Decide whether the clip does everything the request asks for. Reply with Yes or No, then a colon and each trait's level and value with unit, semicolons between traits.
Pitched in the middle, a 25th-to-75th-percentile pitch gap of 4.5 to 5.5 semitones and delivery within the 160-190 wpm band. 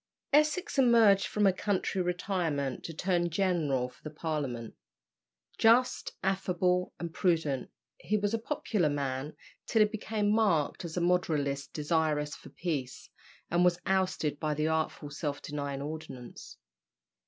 No: medium, 170 Hz; average, 4.8 semitones; average, 140 wpm